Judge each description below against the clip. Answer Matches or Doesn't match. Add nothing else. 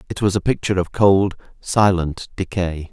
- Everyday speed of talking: Matches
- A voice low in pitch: Matches